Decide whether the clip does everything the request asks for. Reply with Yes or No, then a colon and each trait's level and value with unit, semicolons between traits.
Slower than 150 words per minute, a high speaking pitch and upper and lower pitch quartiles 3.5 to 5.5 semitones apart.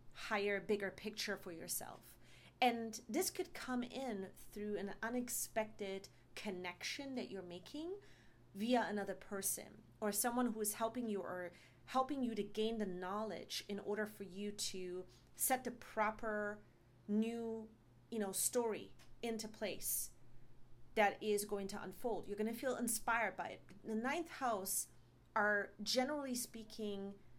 No: average, 140 wpm; high, 210 Hz; average, 3.0 semitones